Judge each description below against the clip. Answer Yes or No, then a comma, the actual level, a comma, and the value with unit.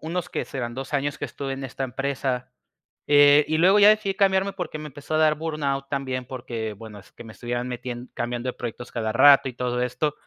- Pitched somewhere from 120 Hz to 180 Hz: Yes, low, 135 Hz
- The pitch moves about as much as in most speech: Yes, average, 3.7 semitones